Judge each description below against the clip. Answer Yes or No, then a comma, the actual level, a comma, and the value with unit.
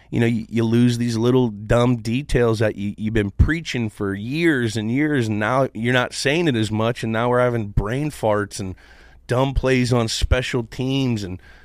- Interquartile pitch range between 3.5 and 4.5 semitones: No, average, 2.9 semitones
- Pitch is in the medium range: No, low, 120 Hz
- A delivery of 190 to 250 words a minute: Yes, average, 200 wpm